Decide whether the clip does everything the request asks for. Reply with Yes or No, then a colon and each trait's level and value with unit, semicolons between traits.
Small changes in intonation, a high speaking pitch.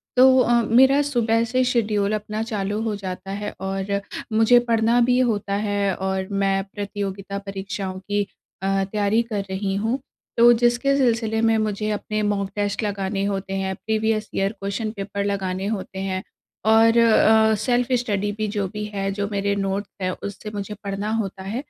Yes: narrow, 2.3 semitones; high, 205 Hz